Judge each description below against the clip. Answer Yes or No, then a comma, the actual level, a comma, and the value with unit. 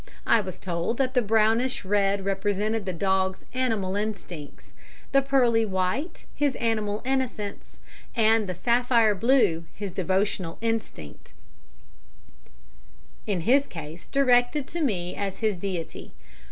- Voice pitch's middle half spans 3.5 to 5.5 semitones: Yes, average, 4.4 semitones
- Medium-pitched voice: No, high, 210 Hz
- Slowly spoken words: Yes, slow, 125 wpm